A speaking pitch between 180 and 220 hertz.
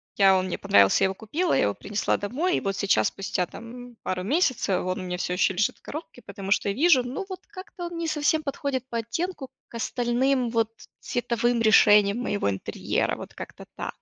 No: high, 235 Hz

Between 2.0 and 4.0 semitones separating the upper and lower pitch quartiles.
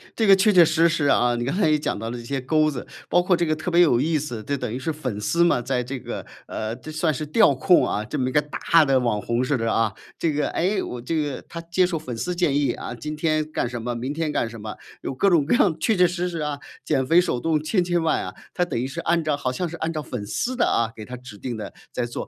No: average, 5.3 semitones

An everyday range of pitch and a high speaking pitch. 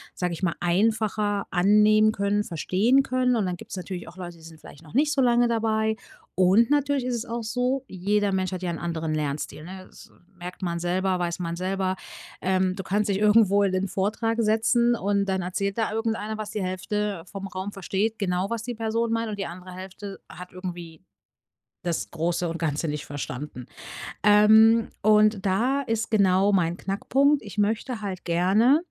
Yes: average, 3.4 semitones; high, 200 Hz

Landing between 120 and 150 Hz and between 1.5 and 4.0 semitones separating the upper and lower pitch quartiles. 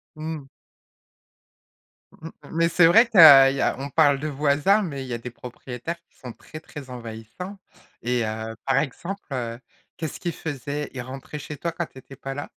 No: medium, 140 Hz; average, 4.4 semitones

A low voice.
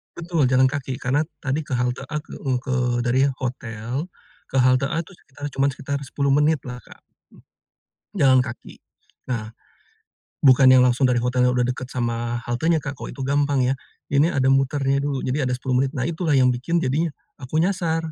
Yes: low, 130 Hz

